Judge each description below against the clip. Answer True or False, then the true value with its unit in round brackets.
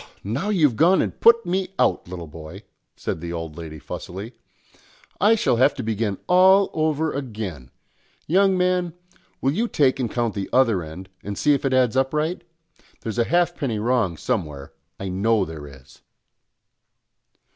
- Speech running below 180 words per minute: True (165 wpm)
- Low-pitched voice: True (120 Hz)